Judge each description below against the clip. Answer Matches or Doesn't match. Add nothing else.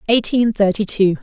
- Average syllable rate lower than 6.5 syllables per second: Matches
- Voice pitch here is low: Doesn't match